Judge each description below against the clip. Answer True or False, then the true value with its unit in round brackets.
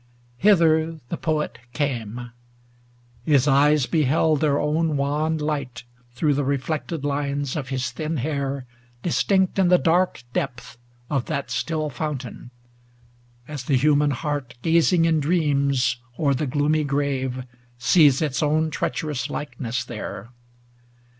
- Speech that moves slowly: True (130 wpm)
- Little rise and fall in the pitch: False (3.0 semitones)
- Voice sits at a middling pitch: True (145 Hz)